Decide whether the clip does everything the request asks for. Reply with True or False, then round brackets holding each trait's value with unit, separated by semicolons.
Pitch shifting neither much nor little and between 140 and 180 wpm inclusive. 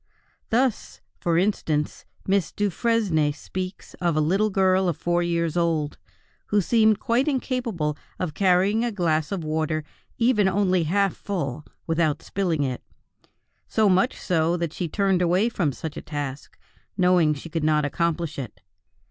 True (4.3 semitones; 150 wpm)